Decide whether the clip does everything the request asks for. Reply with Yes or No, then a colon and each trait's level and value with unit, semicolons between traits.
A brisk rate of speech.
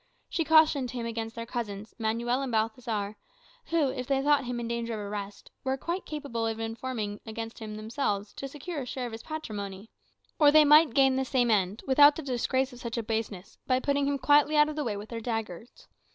Yes: fast, 215 wpm